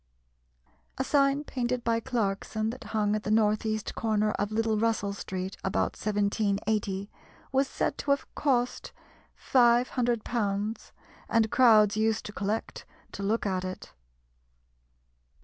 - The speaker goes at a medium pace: No, slow, 130 wpm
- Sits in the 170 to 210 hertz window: No, high, 220 Hz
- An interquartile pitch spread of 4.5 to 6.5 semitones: No, average, 2.7 semitones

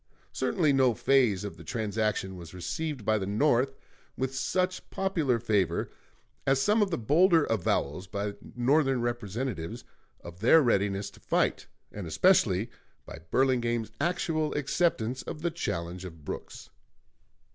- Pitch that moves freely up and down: Yes, wide, 6.6 semitones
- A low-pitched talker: Yes, low, 120 Hz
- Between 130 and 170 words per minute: Yes, slow, 135 wpm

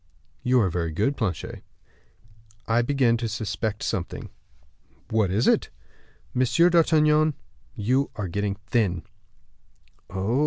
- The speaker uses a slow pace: Yes, slow, 115 wpm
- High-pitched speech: No, low, 110 Hz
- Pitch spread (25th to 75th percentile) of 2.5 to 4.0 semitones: No, average, 4.9 semitones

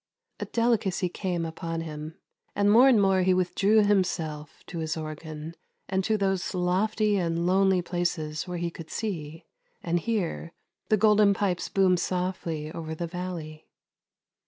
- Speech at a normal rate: Yes, average, 160 wpm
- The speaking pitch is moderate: Yes, medium, 180 Hz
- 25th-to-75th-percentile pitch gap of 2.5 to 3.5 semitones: Yes, average, 3.1 semitones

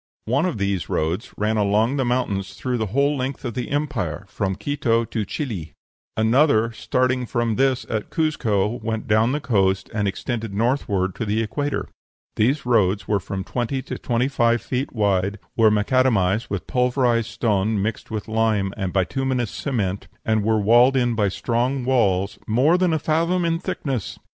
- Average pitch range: Yes, average, 4.1 semitones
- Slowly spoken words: No, average, 170 wpm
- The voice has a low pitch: Yes, low, 115 Hz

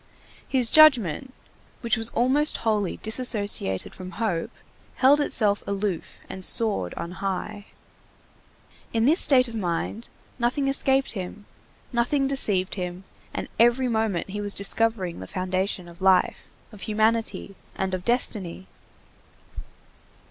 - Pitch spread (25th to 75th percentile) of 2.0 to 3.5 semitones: No, average, 4.3 semitones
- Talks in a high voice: Yes, high, 215 Hz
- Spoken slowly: Yes, slow, 125 wpm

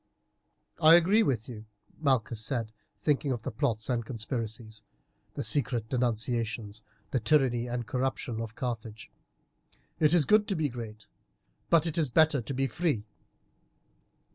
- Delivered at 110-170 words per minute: Yes, average, 140 wpm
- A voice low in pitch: Yes, low, 125 Hz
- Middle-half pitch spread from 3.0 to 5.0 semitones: Yes, average, 4.7 semitones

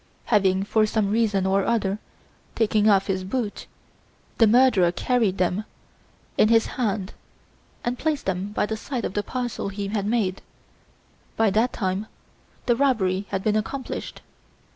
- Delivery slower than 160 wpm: Yes, average, 150 wpm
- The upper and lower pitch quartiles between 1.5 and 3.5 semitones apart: Yes, average, 3.1 semitones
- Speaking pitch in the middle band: No, high, 210 Hz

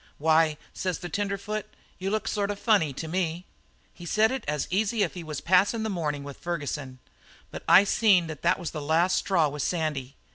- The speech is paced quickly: Yes, fast, 210 wpm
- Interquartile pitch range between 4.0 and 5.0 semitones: Yes, average, 4.6 semitones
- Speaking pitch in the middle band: Yes, medium, 175 Hz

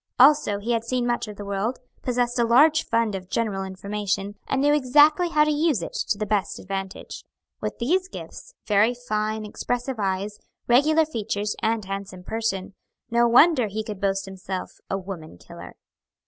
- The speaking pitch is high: Yes, high, 220 Hz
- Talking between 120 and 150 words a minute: No, average, 175 wpm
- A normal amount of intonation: Yes, average, 4.2 semitones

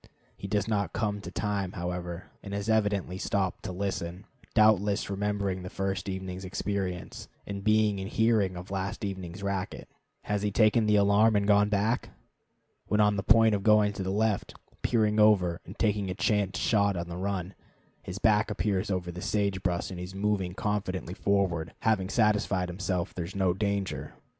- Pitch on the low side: Yes, low, 100 Hz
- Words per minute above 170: Yes, average, 180 wpm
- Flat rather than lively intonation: Yes, narrow, 2.1 semitones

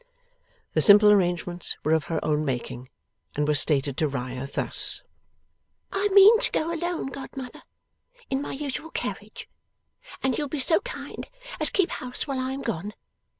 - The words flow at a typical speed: Yes, average, 160 wpm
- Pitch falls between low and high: No, high, 235 Hz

